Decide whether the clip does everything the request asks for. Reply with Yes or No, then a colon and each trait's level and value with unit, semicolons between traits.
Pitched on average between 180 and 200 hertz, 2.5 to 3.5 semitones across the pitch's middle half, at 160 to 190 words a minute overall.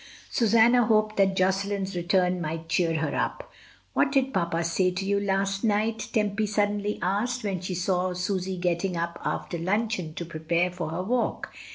Yes: high, 190 Hz; average, 3.0 semitones; average, 170 wpm